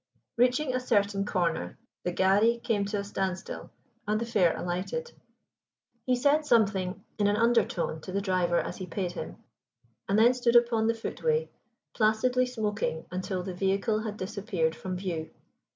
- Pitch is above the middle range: Yes, high, 205 Hz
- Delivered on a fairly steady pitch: No, average, 4.2 semitones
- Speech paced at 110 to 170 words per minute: Yes, average, 160 wpm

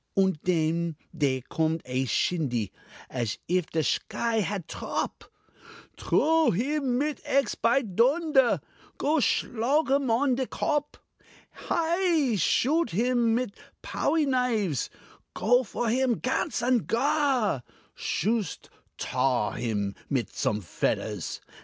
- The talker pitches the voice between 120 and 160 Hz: No, high, 230 Hz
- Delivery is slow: Yes, slow, 120 wpm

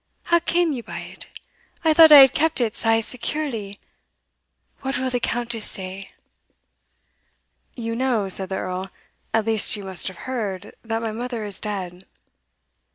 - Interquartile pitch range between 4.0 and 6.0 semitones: Yes, average, 4.7 semitones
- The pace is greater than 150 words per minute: Yes, average, 160 wpm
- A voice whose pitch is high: Yes, high, 225 Hz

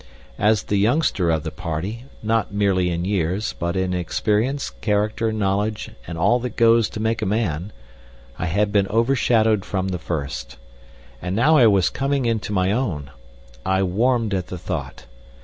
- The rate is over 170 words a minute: No, average, 165 wpm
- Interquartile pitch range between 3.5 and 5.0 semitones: Yes, average, 3.9 semitones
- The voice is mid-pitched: No, low, 100 Hz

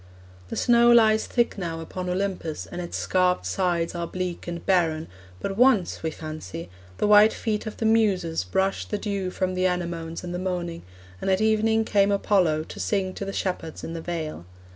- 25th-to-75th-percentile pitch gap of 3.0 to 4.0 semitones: Yes, average, 3.5 semitones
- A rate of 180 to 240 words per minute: Yes, average, 190 wpm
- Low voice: No, medium, 185 Hz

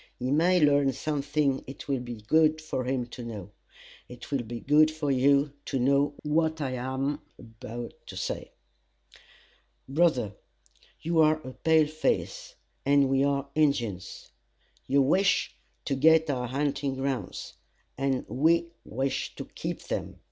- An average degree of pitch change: Yes, average, 3.1 semitones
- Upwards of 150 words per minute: No, average, 145 wpm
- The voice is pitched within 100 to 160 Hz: Yes, medium, 140 Hz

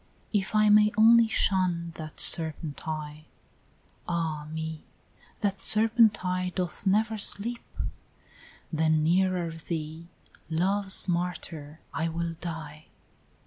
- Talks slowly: Yes, slow, 115 wpm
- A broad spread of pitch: No, average, 4.0 semitones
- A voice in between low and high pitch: Yes, medium, 170 Hz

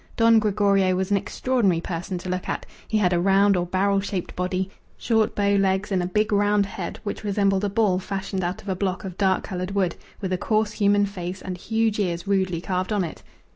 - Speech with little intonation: Yes, narrow, 1.9 semitones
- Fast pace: Yes, fast, 220 wpm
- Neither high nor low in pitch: No, high, 195 Hz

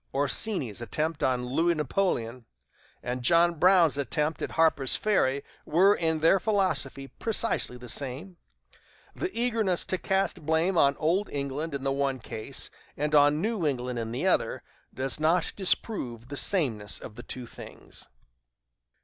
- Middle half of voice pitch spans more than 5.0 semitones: Yes, wide, 5.5 semitones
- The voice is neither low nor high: Yes, medium, 150 Hz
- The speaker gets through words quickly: No, average, 150 wpm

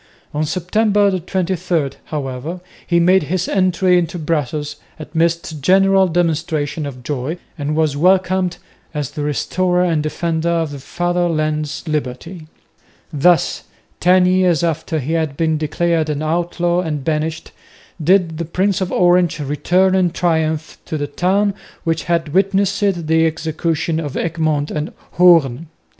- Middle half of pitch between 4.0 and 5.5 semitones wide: No, average, 2.8 semitones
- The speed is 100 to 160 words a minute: Yes, average, 140 wpm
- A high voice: No, medium, 165 Hz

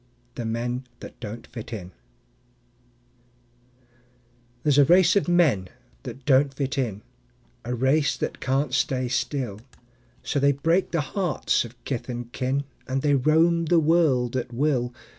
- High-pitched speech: No, low, 135 Hz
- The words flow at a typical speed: Yes, average, 145 wpm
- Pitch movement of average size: Yes, average, 3.8 semitones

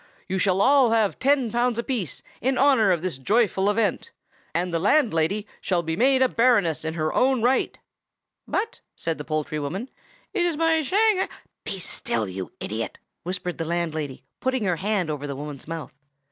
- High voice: Yes, high, 195 Hz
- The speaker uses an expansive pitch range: Yes, wide, 7.9 semitones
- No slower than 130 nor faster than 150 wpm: No, average, 175 wpm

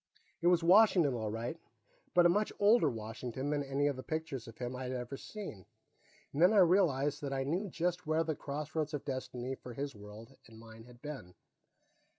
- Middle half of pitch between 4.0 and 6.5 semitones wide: Yes, average, 5.2 semitones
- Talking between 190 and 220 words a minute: Yes, average, 195 wpm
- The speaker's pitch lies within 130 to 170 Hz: Yes, medium, 140 Hz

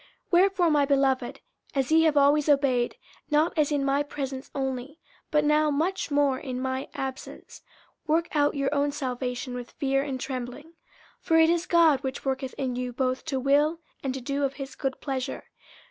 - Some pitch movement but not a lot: No, narrow, 2.3 semitones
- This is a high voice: Yes, very high, 275 Hz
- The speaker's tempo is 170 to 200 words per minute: Yes, average, 190 wpm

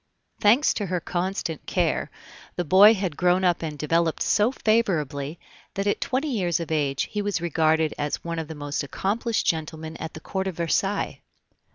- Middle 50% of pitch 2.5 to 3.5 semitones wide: No, average, 4.1 semitones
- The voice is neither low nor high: Yes, medium, 170 Hz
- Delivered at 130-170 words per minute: No, average, 180 wpm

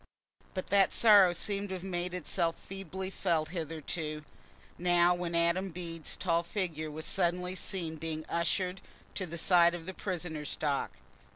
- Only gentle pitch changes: Yes, narrow, 2.3 semitones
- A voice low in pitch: No, medium, 175 Hz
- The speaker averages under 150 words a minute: No, average, 160 wpm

